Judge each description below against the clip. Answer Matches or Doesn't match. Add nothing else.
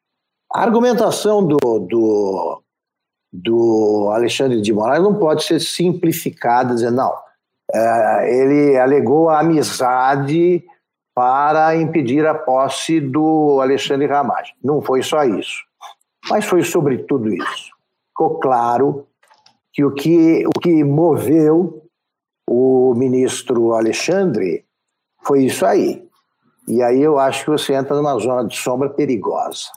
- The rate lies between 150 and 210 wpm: Doesn't match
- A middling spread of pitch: Matches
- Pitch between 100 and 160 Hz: Matches